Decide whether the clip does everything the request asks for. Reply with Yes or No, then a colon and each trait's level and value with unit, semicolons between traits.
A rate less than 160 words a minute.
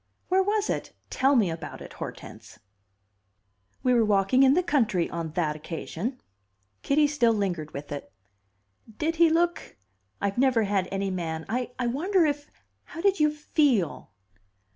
Yes: average, 150 wpm